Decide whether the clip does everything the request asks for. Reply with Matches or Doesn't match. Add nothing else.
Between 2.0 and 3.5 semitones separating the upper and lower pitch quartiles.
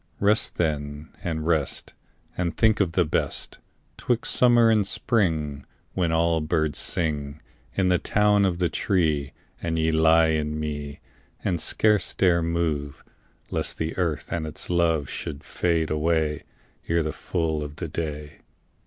Matches